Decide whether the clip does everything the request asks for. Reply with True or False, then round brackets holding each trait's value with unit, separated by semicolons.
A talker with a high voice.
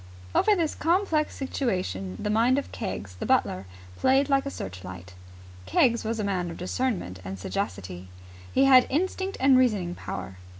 True (220 Hz)